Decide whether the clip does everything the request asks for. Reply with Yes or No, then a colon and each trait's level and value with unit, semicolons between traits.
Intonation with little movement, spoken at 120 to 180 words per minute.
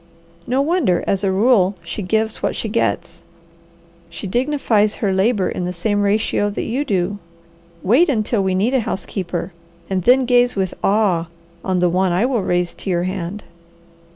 No: average, 4.0 semitones; average, 175 wpm